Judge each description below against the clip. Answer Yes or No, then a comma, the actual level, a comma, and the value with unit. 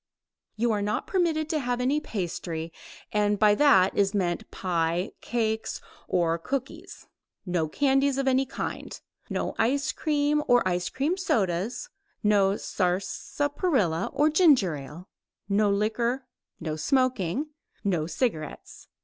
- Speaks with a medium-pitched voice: No, high, 215 Hz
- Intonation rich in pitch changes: Yes, wide, 7.3 semitones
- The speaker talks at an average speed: No, slow, 125 wpm